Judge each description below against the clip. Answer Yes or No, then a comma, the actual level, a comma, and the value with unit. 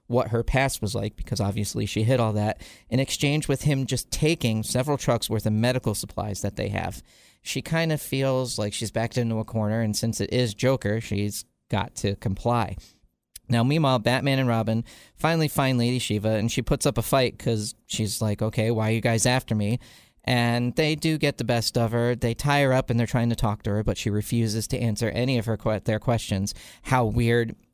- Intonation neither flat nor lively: Yes, average, 3.0 semitones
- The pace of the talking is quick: Yes, fast, 220 wpm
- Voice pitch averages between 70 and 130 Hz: Yes, low, 115 Hz